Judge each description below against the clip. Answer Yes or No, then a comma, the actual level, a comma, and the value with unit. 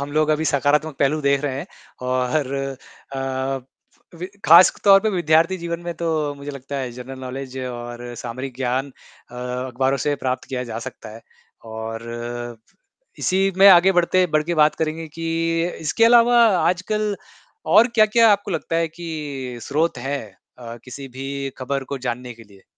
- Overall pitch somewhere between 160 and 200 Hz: No, medium, 145 Hz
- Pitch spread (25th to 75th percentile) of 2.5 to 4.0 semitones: No, average, 4.8 semitones